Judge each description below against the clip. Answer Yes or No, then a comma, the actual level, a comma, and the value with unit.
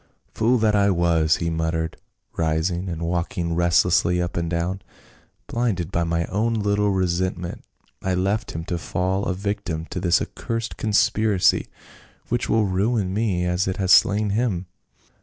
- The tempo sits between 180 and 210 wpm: No, average, 160 wpm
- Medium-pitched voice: No, very low, 95 Hz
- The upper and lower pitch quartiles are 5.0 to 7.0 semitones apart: No, average, 3.3 semitones